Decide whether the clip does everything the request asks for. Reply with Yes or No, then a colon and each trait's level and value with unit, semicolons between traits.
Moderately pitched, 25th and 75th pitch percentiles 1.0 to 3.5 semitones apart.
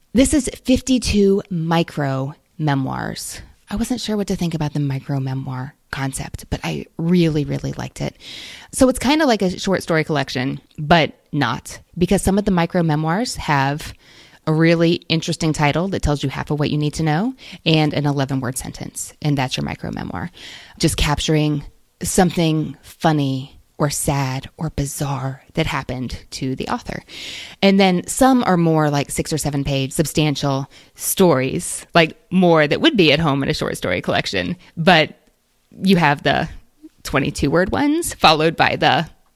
No: medium, 155 Hz; average, 4.4 semitones